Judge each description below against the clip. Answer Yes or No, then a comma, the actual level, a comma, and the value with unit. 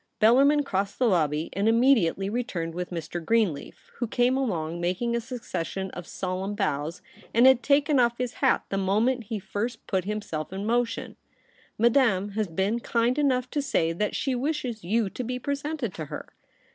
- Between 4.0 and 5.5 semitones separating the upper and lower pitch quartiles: Yes, average, 5.2 semitones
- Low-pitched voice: No, high, 220 Hz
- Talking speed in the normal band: Yes, average, 185 wpm